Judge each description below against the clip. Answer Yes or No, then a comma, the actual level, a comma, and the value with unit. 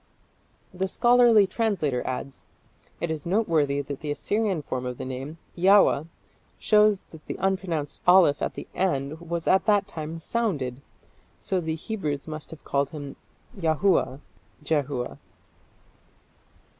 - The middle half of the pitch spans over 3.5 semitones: Yes, average, 5.1 semitones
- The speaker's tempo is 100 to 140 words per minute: Yes, slow, 135 wpm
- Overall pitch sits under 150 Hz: No, medium, 160 Hz